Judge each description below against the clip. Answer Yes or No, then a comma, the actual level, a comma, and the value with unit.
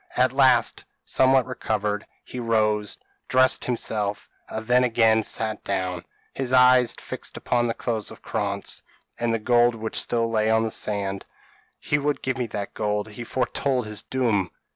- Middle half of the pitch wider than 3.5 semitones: No, average, 2.9 semitones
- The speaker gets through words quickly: No, average, 165 wpm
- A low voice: Yes, low, 115 Hz